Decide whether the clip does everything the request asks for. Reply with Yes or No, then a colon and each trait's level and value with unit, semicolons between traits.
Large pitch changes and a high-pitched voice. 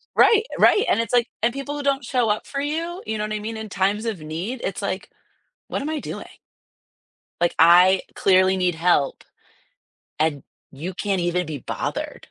Yes: wide, 6.1 semitones; high, 210 Hz